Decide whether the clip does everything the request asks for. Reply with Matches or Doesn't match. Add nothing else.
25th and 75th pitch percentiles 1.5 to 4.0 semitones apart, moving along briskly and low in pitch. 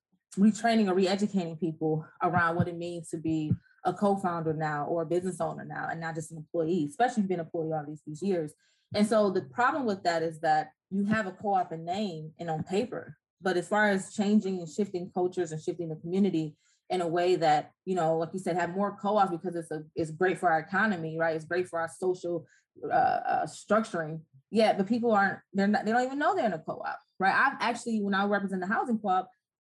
Doesn't match